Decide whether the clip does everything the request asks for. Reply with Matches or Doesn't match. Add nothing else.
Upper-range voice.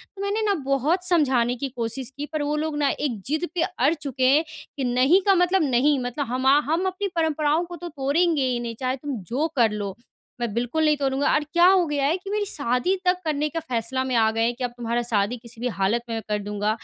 Matches